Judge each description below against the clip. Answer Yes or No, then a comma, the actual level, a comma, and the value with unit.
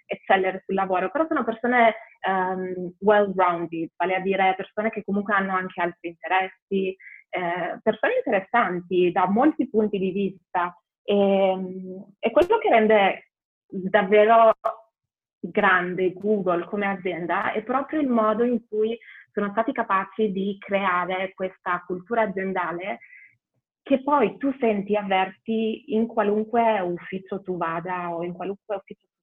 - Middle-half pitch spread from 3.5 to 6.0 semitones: No, average, 2.9 semitones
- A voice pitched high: Yes, high, 195 Hz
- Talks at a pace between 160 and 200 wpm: No, average, 130 wpm